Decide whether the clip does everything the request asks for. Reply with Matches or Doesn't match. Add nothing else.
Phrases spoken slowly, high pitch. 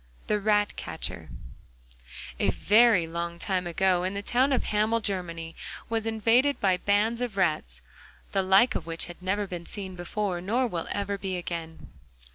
Doesn't match